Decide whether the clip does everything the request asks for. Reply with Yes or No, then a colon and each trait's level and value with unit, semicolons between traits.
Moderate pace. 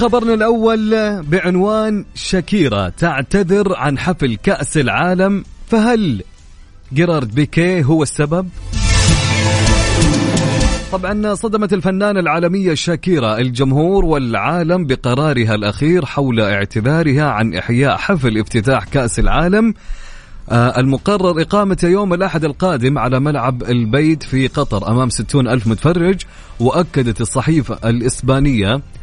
Yes: average, 100 wpm